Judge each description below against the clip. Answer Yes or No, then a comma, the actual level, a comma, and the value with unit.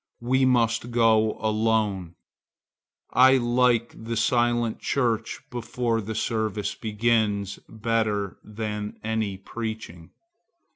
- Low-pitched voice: Yes, low, 110 Hz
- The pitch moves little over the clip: Yes, narrow, 1.8 semitones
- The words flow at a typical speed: No, slow, 95 wpm